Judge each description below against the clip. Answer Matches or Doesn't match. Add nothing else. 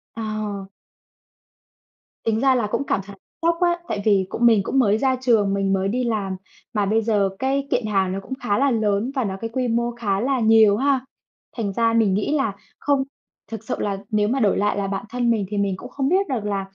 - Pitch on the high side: Matches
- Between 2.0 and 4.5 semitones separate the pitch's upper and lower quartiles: Matches